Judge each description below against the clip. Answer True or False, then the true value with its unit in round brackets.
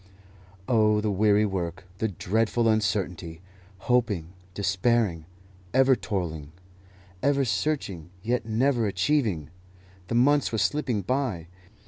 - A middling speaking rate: False (105 wpm)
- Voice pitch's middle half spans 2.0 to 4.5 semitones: False (5.0 semitones)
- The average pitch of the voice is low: True (105 Hz)